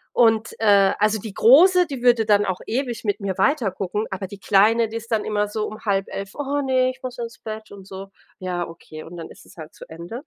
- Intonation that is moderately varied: Yes, average, 3.5 semitones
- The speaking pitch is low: No, high, 215 Hz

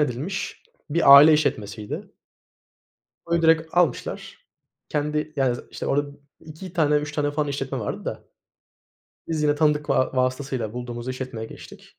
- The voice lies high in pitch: No, medium, 145 Hz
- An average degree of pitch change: Yes, average, 3.2 semitones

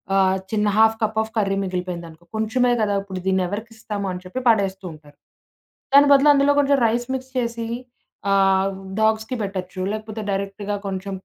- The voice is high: Yes, high, 205 Hz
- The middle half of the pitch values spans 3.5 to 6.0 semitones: No, average, 2.8 semitones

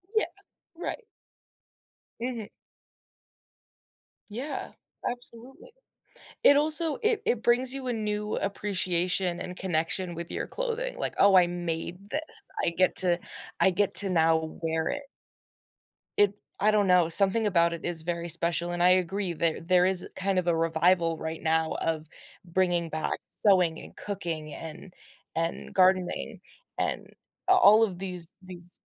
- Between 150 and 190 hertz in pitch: Yes, medium, 185 Hz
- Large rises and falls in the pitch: No, average, 3.7 semitones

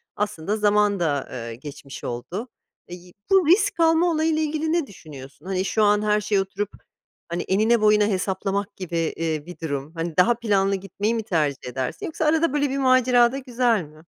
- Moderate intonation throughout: No, wide, 6.8 semitones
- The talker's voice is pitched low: No, high, 205 Hz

